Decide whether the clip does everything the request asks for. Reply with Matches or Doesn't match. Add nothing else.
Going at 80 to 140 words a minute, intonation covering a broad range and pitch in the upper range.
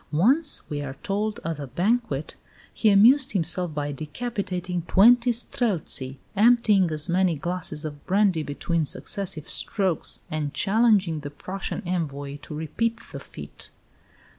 Doesn't match